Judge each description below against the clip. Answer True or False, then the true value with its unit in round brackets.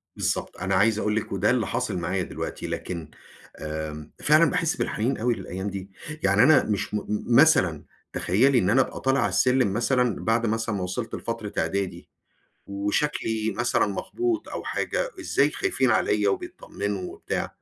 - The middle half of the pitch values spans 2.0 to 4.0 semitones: False (4.5 semitones)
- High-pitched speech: False (110 Hz)